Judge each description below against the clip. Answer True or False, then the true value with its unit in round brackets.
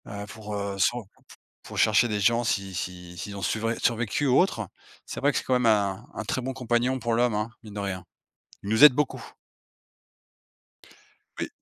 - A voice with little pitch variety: False (3.3 semitones)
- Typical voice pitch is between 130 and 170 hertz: False (110 Hz)